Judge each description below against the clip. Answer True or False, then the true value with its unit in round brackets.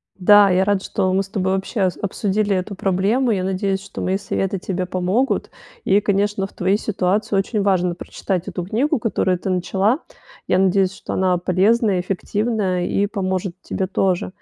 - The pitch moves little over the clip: True (1.7 semitones)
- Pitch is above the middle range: True (195 Hz)